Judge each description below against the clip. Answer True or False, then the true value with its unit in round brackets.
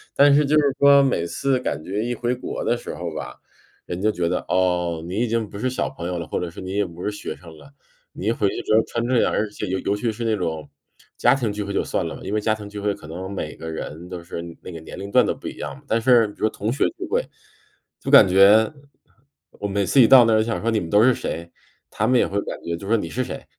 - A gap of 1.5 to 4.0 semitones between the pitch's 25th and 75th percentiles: False (4.9 semitones)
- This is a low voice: True (105 Hz)